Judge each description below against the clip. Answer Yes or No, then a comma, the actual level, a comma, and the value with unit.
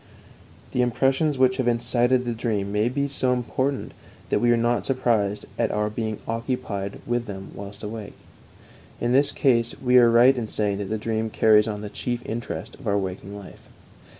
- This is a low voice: Yes, low, 115 Hz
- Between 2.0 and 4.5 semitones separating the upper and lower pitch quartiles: Yes, average, 3.1 semitones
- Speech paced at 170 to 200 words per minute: Yes, average, 185 wpm